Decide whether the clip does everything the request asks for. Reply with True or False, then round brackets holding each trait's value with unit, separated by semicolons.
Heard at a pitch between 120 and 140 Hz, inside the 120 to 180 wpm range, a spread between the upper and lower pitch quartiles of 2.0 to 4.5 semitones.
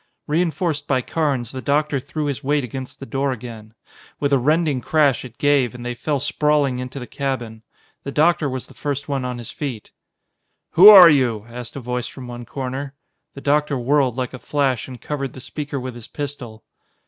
False (135 Hz; 195 wpm; 2.8 semitones)